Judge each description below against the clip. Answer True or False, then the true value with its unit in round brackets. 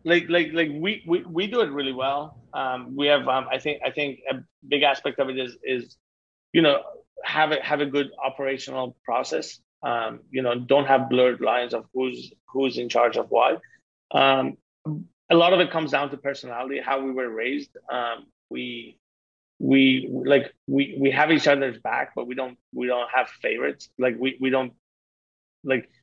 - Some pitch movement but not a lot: False (2.3 semitones)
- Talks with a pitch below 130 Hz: False (135 Hz)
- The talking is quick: False (190 wpm)